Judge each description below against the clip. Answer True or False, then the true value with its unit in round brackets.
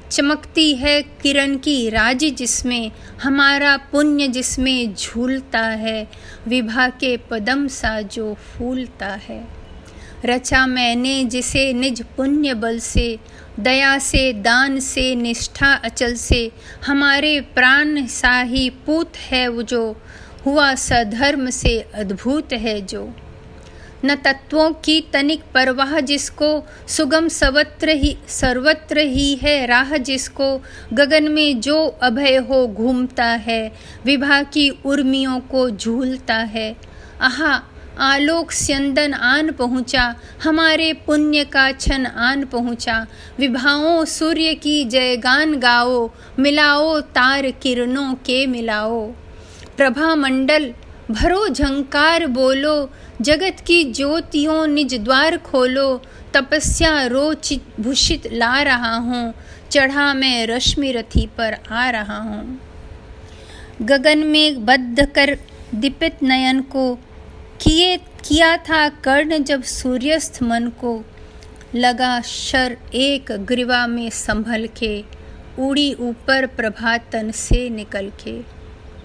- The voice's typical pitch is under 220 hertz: False (265 Hz)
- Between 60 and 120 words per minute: True (110 wpm)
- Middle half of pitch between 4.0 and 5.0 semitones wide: False (3.2 semitones)